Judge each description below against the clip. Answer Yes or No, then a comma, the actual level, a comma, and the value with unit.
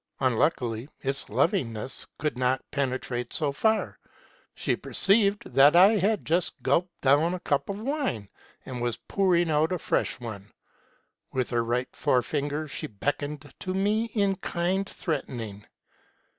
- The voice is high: No, medium, 145 Hz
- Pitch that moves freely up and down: Yes, wide, 6.8 semitones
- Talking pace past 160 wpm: No, average, 145 wpm